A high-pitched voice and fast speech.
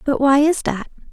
Yes: very high, 280 Hz; fast, 215 wpm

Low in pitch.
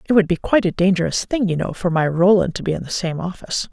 No: medium, 180 Hz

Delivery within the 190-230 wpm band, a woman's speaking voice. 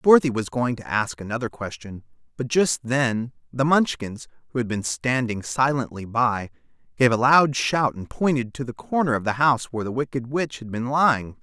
No: average, 195 wpm; male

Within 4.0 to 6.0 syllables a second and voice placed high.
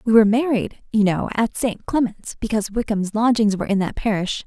Yes: 5.8 syllables/s; high, 215 Hz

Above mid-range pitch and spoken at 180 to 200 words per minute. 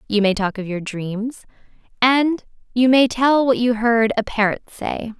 Yes: high, 230 Hz; average, 185 wpm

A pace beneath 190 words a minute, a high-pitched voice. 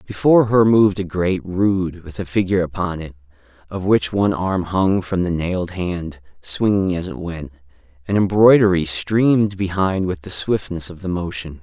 No: average, 175 wpm; very low, 90 Hz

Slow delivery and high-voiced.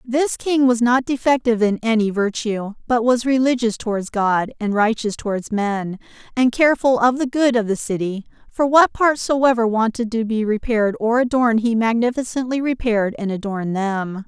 No: average, 170 wpm; high, 230 Hz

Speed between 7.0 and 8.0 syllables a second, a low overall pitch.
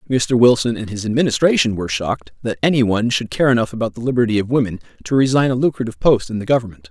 Yes: 7.3 syllables/s; low, 120 Hz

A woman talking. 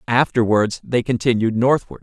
No: male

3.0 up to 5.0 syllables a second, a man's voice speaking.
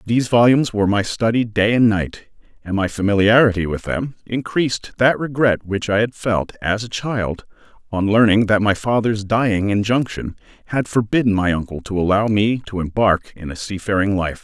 No: 5.2 syllables/s; male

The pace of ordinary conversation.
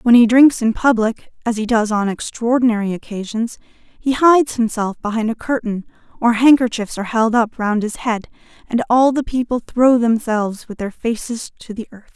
Yes: average, 185 wpm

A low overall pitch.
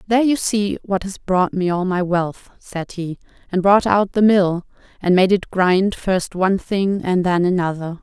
No: high, 190 Hz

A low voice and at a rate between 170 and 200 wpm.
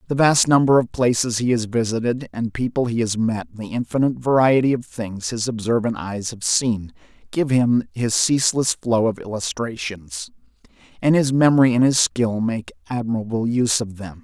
Yes: low, 120 Hz; average, 175 wpm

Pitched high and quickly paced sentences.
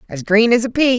Yes: high, 230 Hz; fast, 305 wpm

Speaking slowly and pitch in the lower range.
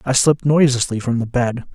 No: fast, 205 wpm; low, 130 Hz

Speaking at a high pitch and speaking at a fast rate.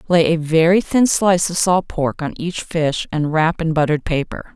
No: medium, 165 Hz; fast, 210 wpm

